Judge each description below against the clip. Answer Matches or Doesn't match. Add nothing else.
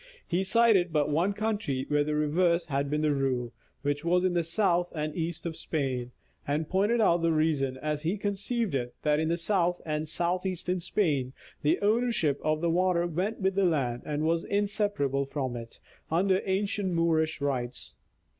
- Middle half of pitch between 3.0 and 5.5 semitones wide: Matches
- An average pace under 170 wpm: Doesn't match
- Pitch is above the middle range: Doesn't match